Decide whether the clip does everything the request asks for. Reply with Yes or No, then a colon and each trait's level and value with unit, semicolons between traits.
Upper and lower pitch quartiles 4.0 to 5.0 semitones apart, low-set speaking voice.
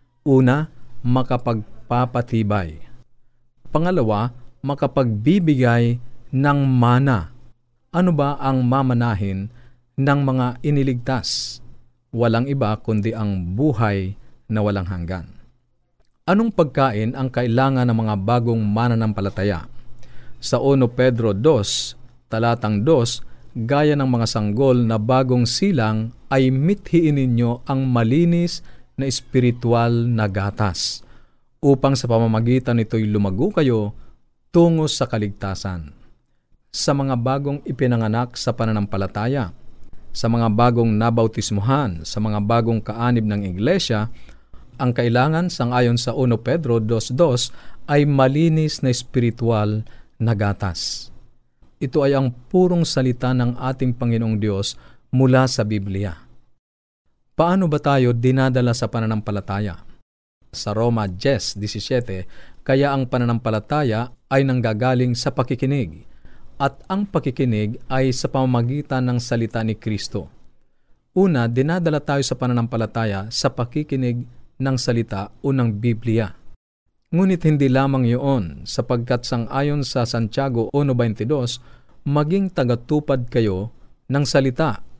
No: average, 3.4 semitones; low, 120 Hz